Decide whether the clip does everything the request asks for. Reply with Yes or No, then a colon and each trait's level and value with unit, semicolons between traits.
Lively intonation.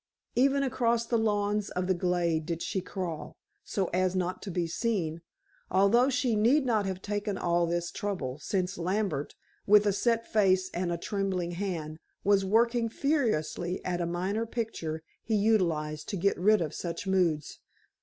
No: average, 3.9 semitones